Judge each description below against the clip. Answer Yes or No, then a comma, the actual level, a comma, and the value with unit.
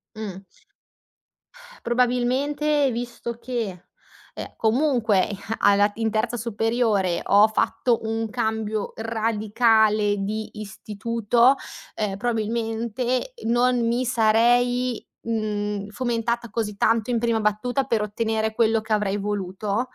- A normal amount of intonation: No, narrow, 2.3 semitones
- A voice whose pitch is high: Yes, high, 225 Hz